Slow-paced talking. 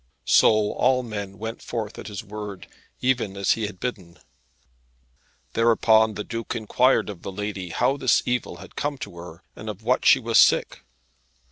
No: average, 170 wpm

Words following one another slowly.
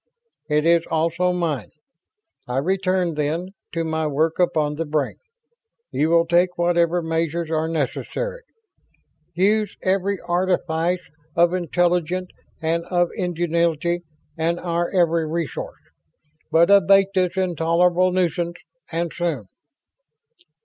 Yes: slow, 115 wpm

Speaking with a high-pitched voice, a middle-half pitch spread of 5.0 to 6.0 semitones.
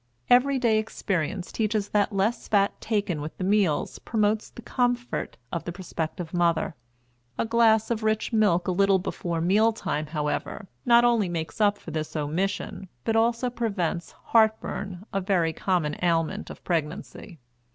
No: high, 195 Hz; average, 4.5 semitones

